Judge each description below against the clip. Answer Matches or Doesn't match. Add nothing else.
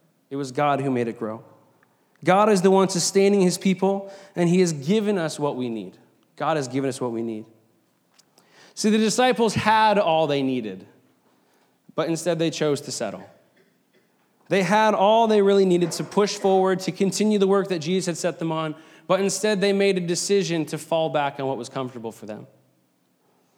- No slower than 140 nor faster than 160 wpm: Doesn't match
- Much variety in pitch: Matches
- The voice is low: Doesn't match